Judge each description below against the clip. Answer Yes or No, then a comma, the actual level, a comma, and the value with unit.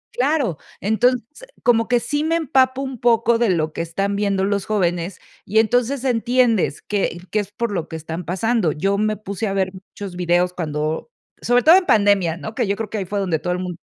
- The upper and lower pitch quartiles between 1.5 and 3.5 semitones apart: No, average, 4.9 semitones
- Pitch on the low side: No, high, 205 Hz